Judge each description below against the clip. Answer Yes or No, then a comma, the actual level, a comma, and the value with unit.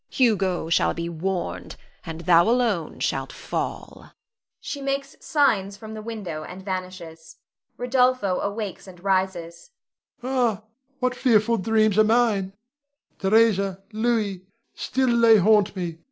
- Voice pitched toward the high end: Yes, high, 200 Hz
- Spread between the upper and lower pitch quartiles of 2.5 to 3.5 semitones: No, average, 4.0 semitones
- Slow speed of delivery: Yes, slow, 125 wpm